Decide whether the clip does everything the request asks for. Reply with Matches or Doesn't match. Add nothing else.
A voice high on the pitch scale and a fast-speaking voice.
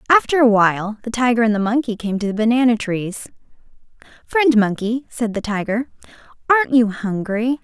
Doesn't match